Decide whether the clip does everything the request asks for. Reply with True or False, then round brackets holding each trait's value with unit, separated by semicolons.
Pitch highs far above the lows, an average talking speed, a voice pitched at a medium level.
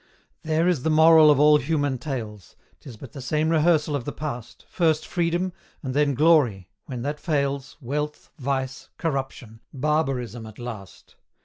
False (3.9 semitones; 155 wpm; 145 Hz)